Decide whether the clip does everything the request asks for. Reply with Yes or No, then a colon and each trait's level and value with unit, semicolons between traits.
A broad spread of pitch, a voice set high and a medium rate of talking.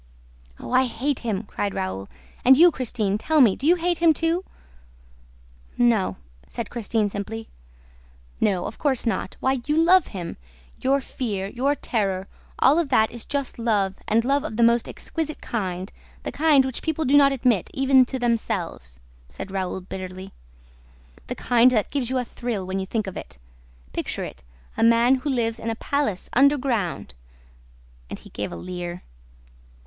Yes: wide, 5.7 semitones; high, 235 Hz; average, 170 wpm